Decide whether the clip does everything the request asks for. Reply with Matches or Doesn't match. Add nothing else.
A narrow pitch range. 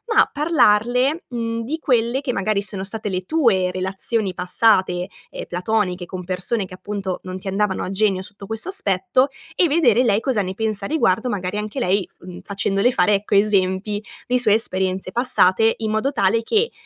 Doesn't match